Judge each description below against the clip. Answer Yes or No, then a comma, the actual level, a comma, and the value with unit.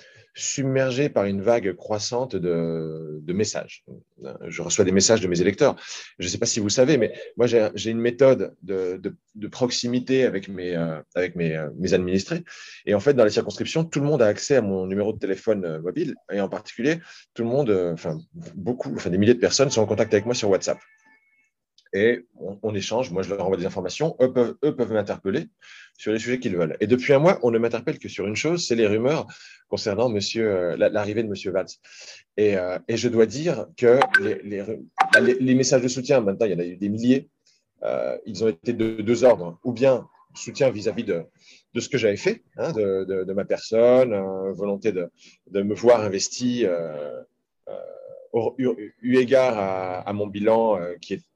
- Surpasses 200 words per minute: Yes, average, 210 wpm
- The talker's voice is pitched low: Yes, low, 115 Hz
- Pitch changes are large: No, average, 4.9 semitones